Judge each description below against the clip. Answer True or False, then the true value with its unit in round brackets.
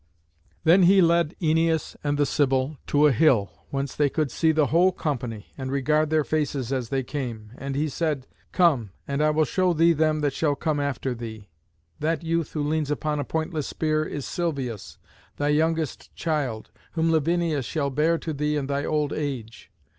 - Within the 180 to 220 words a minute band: True (185 wpm)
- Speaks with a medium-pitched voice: True (150 Hz)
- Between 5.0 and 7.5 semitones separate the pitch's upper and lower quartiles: False (2.8 semitones)